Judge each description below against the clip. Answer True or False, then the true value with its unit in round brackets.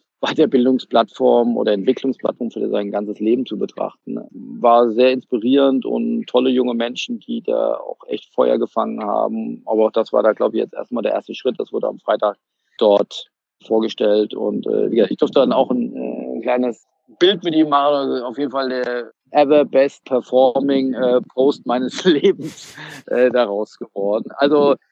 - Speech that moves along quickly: False (175 wpm)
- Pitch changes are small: False (3.0 semitones)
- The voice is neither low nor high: False (130 Hz)